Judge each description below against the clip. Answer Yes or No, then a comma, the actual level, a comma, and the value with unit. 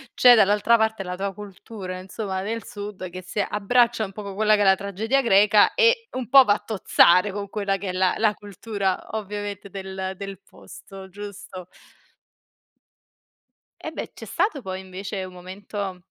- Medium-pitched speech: No, high, 200 Hz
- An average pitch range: No, narrow, 2.1 semitones